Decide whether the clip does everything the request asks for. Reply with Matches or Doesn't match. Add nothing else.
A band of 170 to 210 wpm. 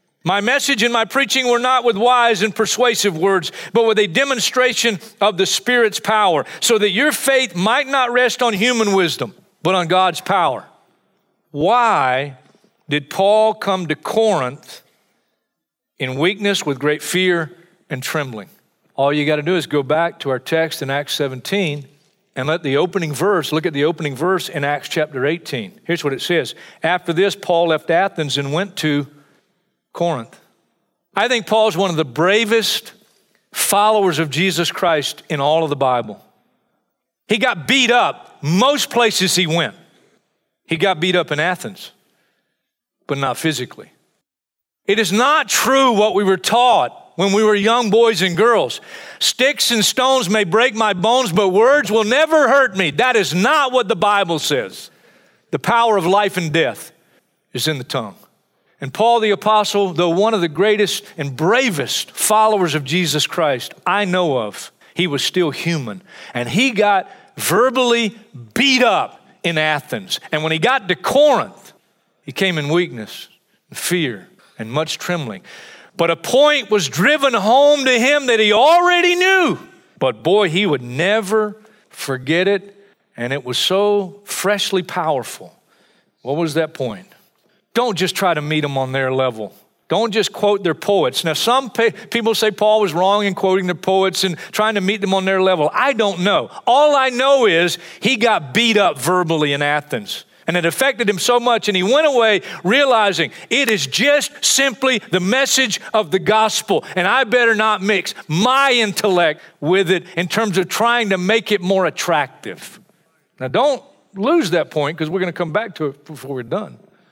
Matches